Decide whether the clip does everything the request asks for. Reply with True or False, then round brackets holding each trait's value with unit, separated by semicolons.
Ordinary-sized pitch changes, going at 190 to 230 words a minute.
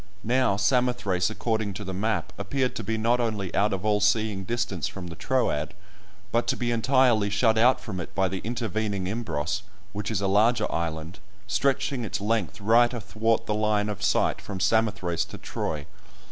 False (3.1 semitones; 180 wpm)